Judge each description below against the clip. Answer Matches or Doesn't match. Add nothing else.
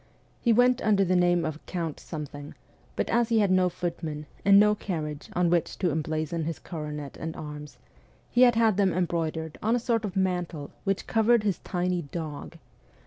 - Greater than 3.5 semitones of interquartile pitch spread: Matches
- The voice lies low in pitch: Doesn't match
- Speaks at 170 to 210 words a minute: Matches